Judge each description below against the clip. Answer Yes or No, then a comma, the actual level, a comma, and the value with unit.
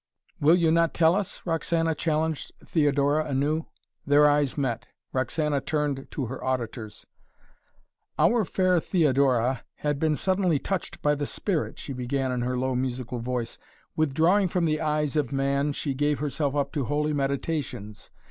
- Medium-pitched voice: Yes, medium, 145 Hz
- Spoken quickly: No, average, 155 wpm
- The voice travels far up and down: No, average, 3.1 semitones